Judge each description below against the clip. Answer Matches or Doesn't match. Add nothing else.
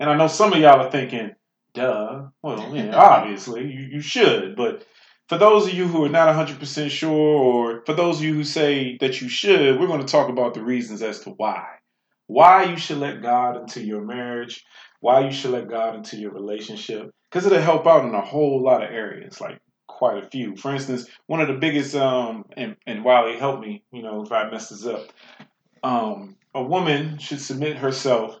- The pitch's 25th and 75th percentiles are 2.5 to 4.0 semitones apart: Doesn't match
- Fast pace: Matches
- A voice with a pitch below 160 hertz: Matches